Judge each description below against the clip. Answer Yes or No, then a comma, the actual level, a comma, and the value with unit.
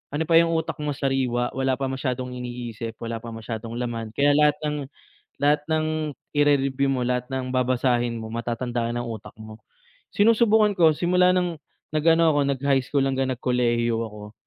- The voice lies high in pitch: No, low, 130 Hz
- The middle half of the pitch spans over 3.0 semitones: Yes, average, 4.0 semitones